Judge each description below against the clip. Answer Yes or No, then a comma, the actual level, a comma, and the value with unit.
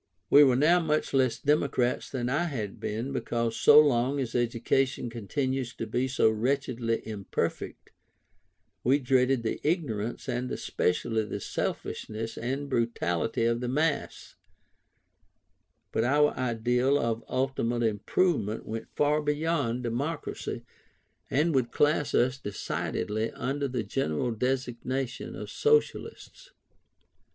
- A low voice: Yes, low, 125 Hz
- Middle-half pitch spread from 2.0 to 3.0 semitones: No, average, 3.5 semitones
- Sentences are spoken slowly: Yes, slow, 120 wpm